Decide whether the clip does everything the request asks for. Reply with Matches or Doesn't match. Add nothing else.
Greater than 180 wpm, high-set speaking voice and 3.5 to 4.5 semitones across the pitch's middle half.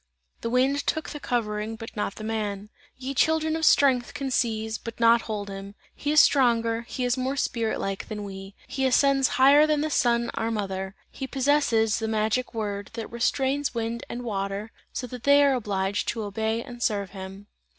Matches